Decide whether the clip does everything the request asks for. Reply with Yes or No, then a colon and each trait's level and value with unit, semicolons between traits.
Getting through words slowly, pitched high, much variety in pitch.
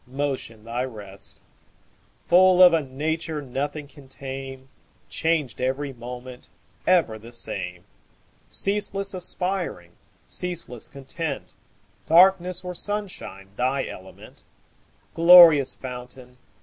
No: slow, 95 wpm; medium, 140 Hz; wide, 5.8 semitones